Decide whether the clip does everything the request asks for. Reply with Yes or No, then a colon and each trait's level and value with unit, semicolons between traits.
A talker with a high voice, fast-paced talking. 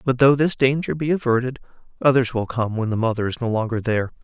No: low, 125 Hz; fast, 225 wpm